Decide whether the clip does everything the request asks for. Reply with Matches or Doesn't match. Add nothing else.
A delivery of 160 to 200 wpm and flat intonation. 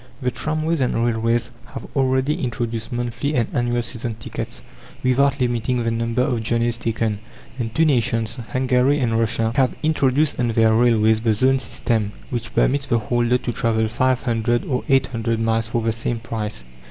Matches